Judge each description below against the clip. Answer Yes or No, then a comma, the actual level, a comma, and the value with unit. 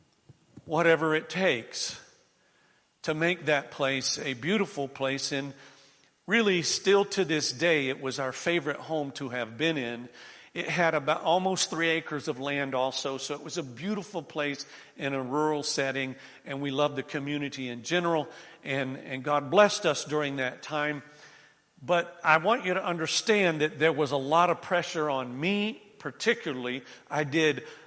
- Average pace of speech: Yes, average, 165 wpm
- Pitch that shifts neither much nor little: Yes, average, 3.7 semitones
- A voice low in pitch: No, medium, 150 Hz